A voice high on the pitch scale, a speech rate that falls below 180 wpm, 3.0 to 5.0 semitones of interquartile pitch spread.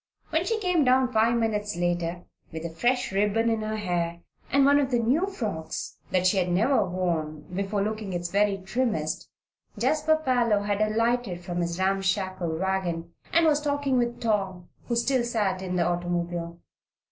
No: high, 205 Hz; average, 170 wpm; wide, 5.5 semitones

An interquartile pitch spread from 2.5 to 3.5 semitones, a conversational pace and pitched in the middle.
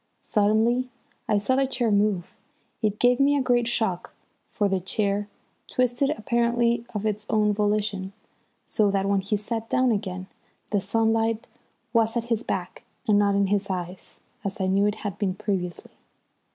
No: average, 2.8 semitones; average, 165 wpm; high, 210 Hz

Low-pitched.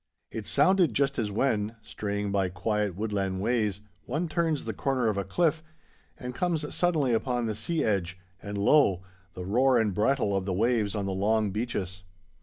Yes: low, 110 Hz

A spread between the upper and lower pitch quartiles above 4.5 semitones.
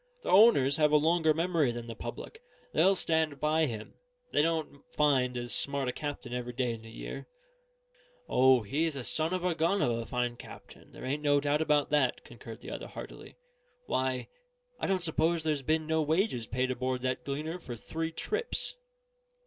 No: average, 4.2 semitones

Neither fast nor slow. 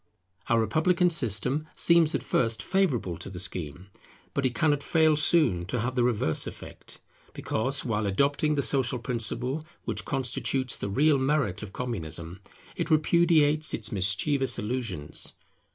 Yes: average, 150 wpm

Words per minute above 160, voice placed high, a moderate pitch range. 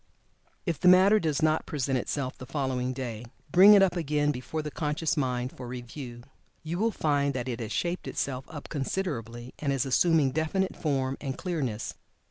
No: average, 180 wpm; medium, 140 Hz; average, 4.1 semitones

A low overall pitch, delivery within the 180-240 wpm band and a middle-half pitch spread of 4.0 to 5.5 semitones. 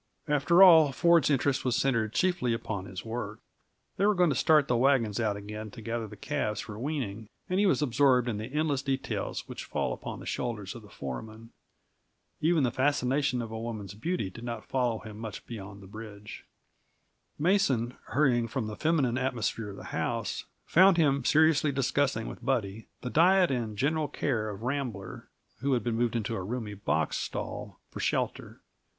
Yes: low, 120 Hz; average, 185 wpm; average, 4.8 semitones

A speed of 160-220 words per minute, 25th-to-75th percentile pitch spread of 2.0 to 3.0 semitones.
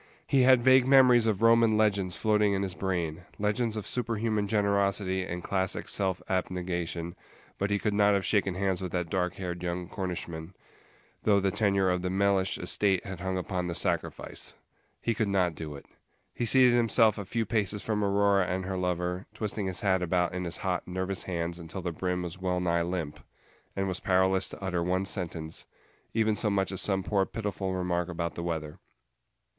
Yes: average, 190 wpm; narrow, 2.5 semitones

